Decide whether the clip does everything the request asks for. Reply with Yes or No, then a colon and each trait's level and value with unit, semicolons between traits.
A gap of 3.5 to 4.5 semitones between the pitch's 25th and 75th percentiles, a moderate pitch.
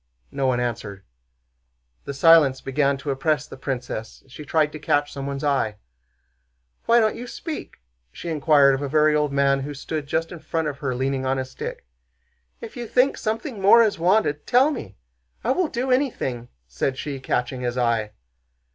Yes: average, 3.9 semitones; medium, 145 Hz